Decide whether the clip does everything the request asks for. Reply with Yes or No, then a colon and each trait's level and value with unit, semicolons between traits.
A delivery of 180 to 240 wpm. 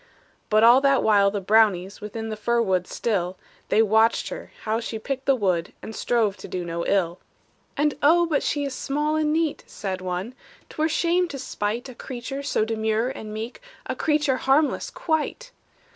Yes: average, 190 wpm